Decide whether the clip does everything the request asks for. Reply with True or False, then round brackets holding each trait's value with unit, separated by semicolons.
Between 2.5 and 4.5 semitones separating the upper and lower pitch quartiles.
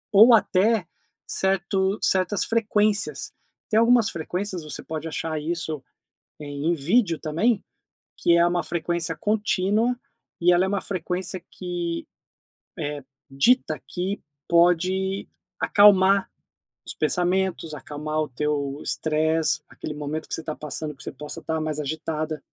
True (3.7 semitones)